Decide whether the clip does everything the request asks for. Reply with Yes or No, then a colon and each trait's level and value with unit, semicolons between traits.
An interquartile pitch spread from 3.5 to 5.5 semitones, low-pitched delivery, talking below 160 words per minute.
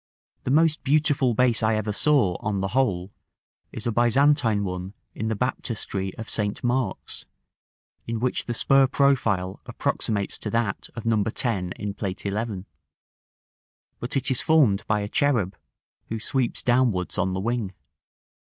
Yes: average, 4.2 semitones; low, 115 Hz; average, 150 wpm